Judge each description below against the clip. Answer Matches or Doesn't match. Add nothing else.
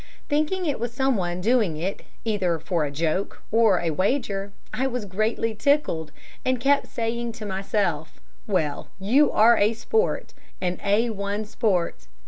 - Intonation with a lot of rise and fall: Doesn't match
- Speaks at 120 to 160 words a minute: Matches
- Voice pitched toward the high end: Matches